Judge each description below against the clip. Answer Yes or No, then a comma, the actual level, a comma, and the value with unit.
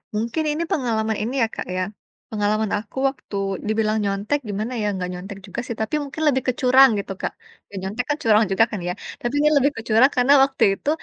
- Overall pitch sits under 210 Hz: No, high, 225 Hz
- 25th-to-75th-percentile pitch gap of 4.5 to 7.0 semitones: No, average, 4.1 semitones